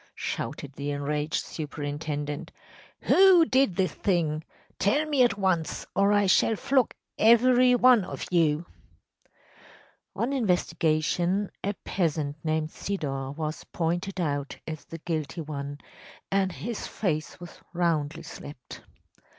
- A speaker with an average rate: No, slow, 125 wpm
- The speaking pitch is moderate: Yes, medium, 170 Hz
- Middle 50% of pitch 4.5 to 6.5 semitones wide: Yes, average, 5.3 semitones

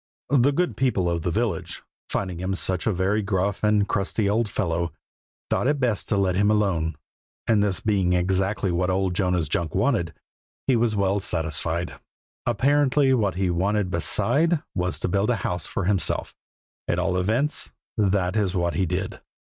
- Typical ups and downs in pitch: Yes, average, 3.2 semitones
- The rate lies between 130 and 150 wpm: No, average, 175 wpm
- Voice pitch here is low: Yes, very low, 95 Hz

